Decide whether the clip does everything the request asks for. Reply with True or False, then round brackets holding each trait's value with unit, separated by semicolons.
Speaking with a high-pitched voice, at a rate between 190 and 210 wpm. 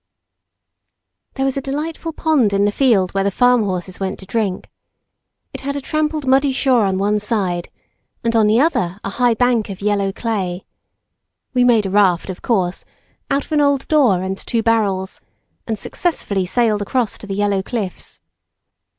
False (215 Hz; 175 wpm)